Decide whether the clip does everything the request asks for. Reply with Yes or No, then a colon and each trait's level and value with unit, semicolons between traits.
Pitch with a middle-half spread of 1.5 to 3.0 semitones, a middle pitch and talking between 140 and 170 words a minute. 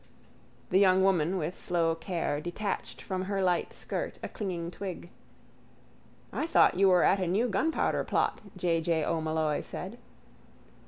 Yes: narrow, 2.6 semitones; medium, 180 Hz; average, 150 wpm